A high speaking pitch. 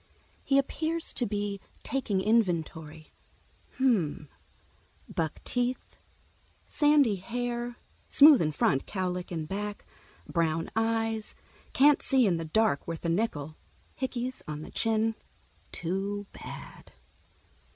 Yes: high, 210 Hz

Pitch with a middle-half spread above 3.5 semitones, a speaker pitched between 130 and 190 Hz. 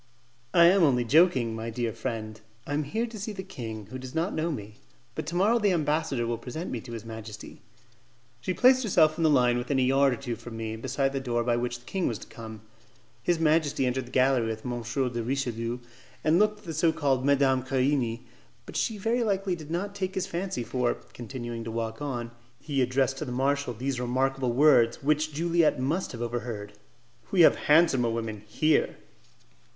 Yes: average, 5.2 semitones; low, 135 Hz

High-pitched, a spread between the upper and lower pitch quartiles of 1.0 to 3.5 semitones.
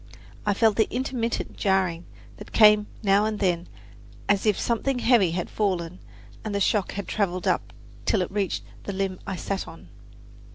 Yes: high, 200 Hz; narrow, 2.6 semitones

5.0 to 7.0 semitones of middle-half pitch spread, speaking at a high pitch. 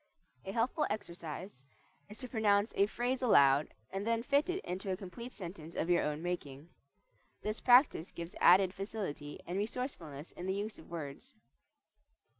Yes: wide, 5.4 semitones; high, 195 Hz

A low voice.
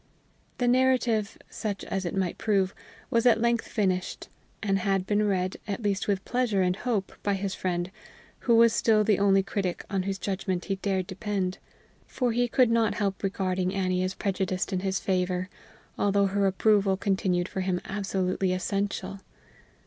No: high, 195 Hz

